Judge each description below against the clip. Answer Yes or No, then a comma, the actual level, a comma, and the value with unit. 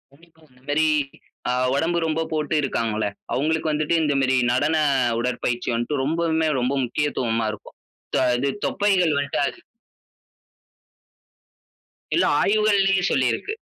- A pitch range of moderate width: Yes, average, 4.2 semitones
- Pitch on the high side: No, medium, 150 Hz